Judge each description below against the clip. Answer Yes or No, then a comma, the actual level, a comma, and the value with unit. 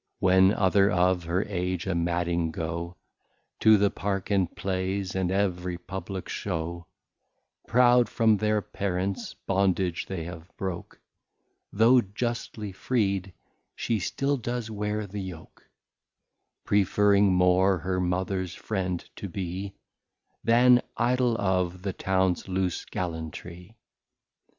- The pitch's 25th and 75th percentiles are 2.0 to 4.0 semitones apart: Yes, narrow, 2.4 semitones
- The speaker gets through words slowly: Yes, slow, 115 wpm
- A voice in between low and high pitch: No, very low, 95 Hz